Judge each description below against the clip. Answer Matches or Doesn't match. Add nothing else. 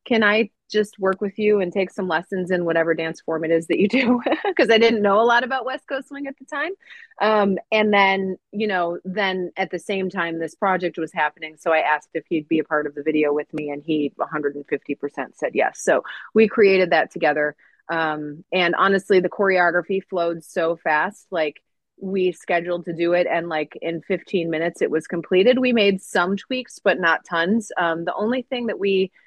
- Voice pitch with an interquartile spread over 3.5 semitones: Matches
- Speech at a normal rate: Doesn't match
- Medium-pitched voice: Matches